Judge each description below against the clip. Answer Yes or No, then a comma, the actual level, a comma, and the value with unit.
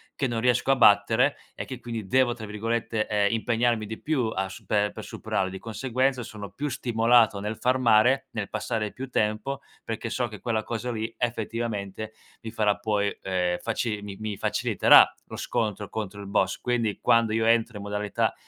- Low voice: Yes, low, 110 Hz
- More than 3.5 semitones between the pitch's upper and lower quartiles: No, narrow, 2.5 semitones